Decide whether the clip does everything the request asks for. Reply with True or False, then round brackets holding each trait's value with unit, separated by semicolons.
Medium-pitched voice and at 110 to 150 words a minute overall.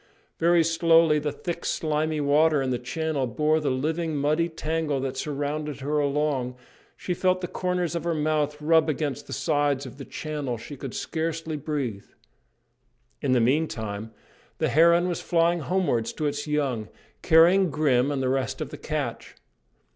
False (150 Hz; 165 wpm)